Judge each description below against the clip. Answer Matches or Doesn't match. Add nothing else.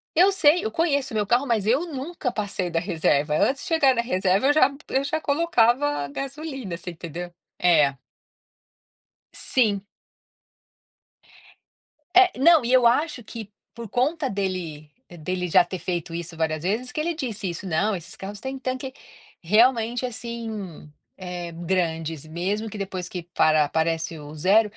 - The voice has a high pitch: Matches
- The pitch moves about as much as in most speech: Doesn't match